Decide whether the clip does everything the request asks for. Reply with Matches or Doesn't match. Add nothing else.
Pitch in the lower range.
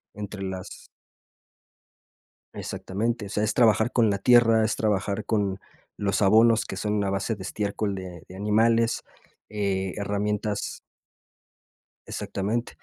Matches